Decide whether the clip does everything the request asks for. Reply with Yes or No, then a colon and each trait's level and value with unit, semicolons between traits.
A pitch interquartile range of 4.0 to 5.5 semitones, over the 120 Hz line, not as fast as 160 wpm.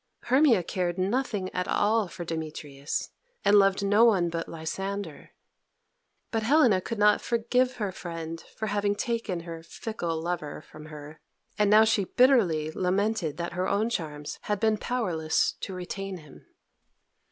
Yes: average, 4.7 semitones; high, 190 Hz; average, 150 wpm